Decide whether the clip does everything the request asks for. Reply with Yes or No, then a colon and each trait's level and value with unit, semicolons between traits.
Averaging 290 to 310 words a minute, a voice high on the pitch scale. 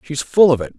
No: fast, 305 wpm; medium, 150 Hz